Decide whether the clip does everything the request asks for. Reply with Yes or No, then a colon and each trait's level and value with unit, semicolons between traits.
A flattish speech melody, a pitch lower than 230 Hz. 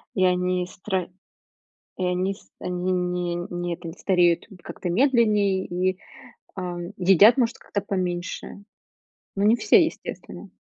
Yes: narrow, 2.0 semitones; medium, 185 Hz